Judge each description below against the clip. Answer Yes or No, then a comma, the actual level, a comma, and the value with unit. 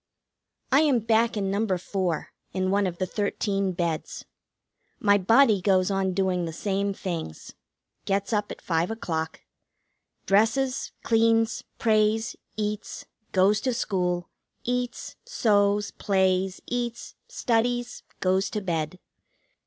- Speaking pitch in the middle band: No, high, 200 Hz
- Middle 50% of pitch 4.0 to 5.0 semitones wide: No, average, 3.3 semitones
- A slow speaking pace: Yes, slow, 120 wpm